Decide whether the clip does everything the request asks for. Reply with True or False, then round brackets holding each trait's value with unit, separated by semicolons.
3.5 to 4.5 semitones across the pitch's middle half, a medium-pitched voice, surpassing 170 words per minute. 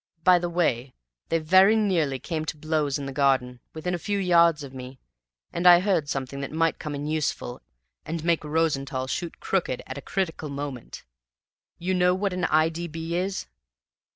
True (3.9 semitones; 160 Hz; 185 wpm)